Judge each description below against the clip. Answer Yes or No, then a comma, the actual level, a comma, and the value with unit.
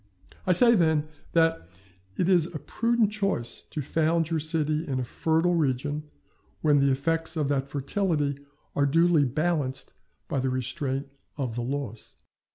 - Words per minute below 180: Yes, average, 155 wpm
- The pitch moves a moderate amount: Yes, average, 3.3 semitones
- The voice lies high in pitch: No, medium, 150 Hz